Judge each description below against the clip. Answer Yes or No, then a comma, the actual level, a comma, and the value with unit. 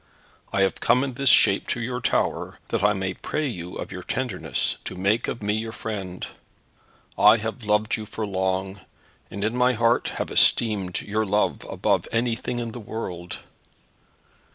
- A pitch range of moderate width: Yes, average, 3.4 semitones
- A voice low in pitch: Yes, low, 105 Hz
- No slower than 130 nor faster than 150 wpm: No, average, 175 wpm